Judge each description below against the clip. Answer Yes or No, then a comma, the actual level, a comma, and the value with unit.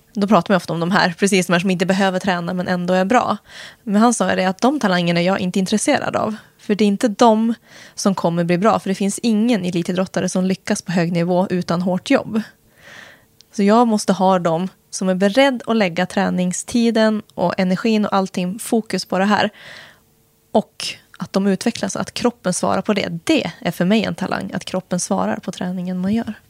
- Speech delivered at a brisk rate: Yes, fast, 210 wpm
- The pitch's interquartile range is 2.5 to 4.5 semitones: Yes, average, 2.8 semitones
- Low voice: No, high, 195 Hz